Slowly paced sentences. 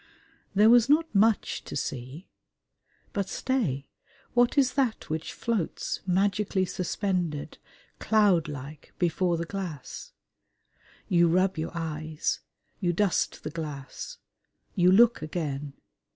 Yes: slow, 110 wpm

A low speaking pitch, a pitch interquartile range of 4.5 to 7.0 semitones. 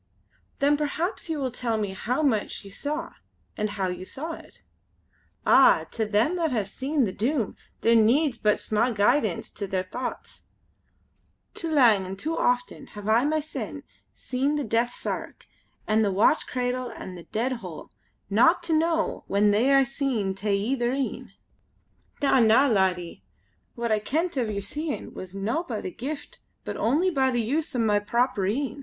No: high, 240 Hz; wide, 5.4 semitones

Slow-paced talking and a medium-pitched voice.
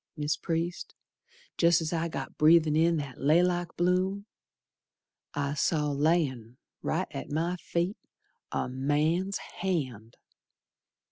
Yes: slow, 110 wpm; medium, 160 Hz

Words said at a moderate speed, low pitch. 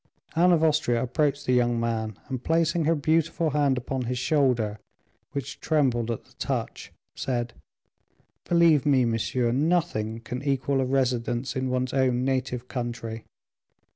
Yes: average, 145 wpm; low, 130 Hz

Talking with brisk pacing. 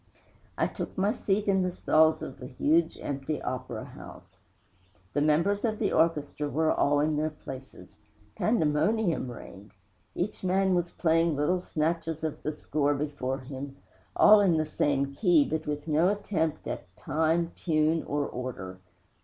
No: average, 155 wpm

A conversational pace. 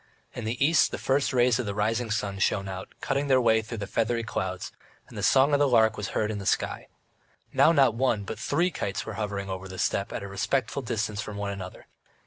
No: fast, 235 wpm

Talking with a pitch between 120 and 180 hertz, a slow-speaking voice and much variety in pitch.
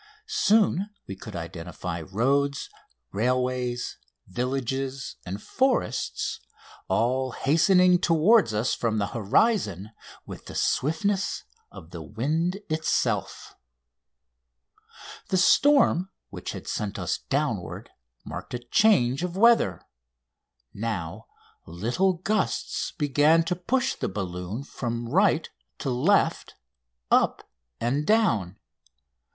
Yes: low, 135 Hz; slow, 100 wpm; wide, 8.6 semitones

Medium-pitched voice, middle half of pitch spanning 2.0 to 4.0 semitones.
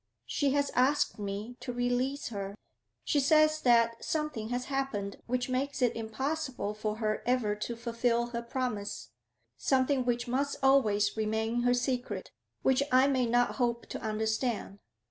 No: high, 245 Hz; average, 3.2 semitones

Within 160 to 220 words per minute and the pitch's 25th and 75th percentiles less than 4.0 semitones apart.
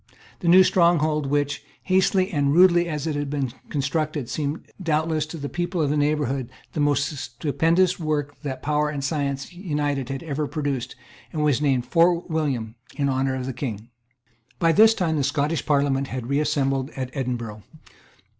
Yes: average, 165 wpm; average, 2.8 semitones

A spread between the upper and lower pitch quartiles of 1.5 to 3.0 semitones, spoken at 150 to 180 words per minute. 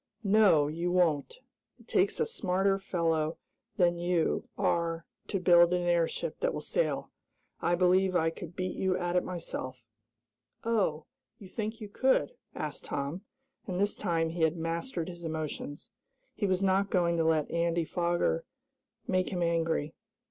Yes: narrow, 2.5 semitones; average, 155 wpm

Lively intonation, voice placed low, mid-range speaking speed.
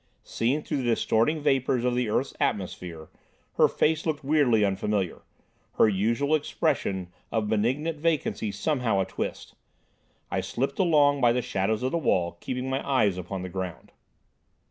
Yes: wide, 6.2 semitones; low, 120 Hz; average, 155 wpm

